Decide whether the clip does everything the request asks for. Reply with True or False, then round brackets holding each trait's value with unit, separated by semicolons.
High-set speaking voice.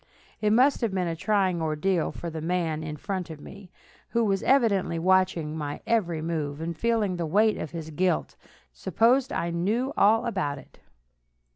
False (180 Hz)